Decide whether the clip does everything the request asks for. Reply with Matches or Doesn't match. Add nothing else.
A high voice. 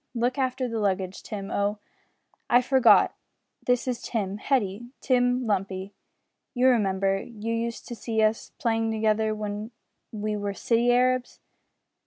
Matches